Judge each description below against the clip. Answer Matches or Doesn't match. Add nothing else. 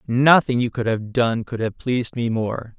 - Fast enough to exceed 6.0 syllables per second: Doesn't match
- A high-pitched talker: Doesn't match